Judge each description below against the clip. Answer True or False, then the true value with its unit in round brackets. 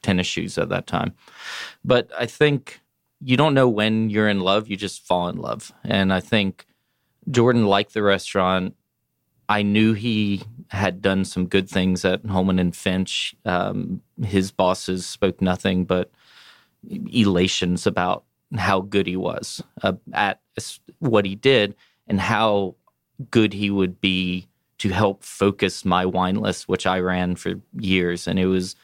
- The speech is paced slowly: False (160 wpm)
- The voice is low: True (95 Hz)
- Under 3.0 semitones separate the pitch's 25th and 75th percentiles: True (2.6 semitones)